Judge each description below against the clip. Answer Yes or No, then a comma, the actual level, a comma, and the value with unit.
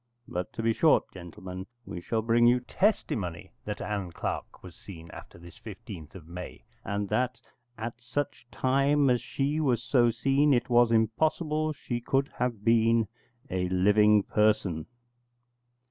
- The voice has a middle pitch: No, low, 115 Hz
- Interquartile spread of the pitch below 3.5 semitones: No, average, 4.9 semitones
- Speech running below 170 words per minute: Yes, average, 150 wpm